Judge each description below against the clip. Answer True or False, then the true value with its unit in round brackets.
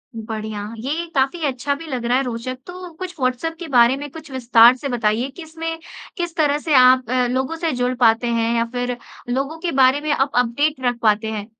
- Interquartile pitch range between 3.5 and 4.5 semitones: True (4.2 semitones)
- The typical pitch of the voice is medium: False (260 Hz)